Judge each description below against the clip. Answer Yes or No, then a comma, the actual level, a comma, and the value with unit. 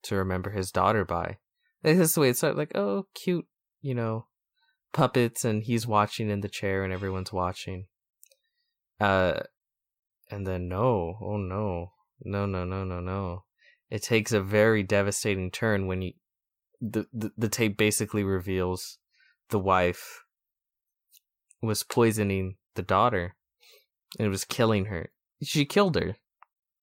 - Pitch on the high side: No, low, 105 Hz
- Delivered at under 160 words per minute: Yes, average, 145 wpm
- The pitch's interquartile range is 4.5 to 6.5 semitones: No, average, 3.7 semitones